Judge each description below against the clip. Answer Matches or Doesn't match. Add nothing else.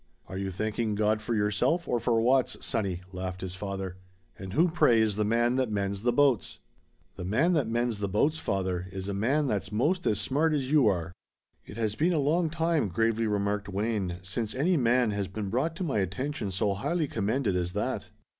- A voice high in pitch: Doesn't match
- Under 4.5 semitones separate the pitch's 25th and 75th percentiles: Doesn't match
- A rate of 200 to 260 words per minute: Matches